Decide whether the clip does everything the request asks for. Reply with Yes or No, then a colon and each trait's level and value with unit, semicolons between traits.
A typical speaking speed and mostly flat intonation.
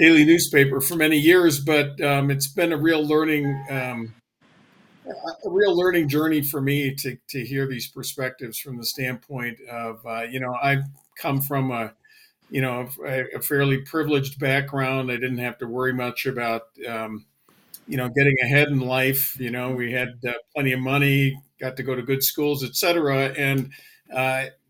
Yes: average, 175 wpm; narrow, 2.2 semitones